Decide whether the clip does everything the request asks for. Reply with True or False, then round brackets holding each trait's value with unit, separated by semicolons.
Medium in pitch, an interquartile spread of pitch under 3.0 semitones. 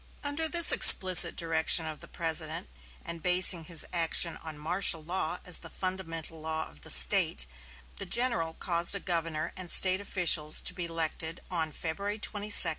True (170 Hz; 2.6 semitones)